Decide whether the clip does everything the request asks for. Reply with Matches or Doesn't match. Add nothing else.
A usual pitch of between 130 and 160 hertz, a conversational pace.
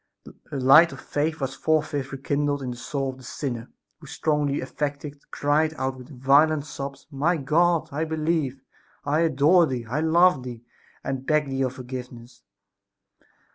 Matches